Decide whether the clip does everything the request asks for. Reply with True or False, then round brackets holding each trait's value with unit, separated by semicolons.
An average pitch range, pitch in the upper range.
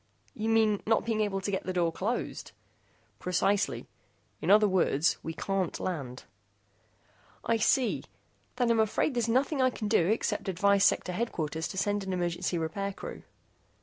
True (3.6 semitones; 200 Hz)